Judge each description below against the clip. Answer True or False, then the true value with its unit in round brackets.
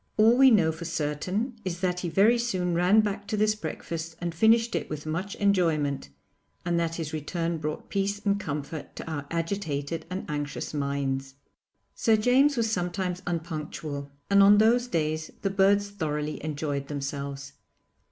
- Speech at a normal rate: True (160 wpm)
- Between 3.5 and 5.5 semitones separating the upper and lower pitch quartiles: True (4.9 semitones)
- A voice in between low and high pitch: True (170 Hz)